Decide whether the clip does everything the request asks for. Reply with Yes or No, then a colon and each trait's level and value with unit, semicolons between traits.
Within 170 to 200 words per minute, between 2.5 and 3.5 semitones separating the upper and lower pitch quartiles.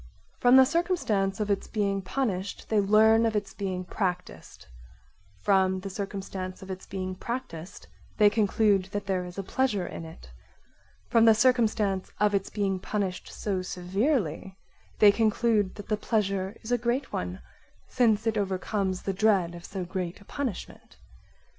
No: average, 160 wpm; average, 2.8 semitones